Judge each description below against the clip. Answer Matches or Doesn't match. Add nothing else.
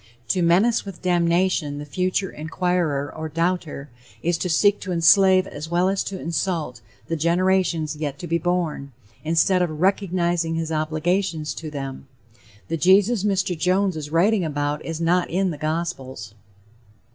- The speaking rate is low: Doesn't match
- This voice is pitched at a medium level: Matches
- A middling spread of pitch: Matches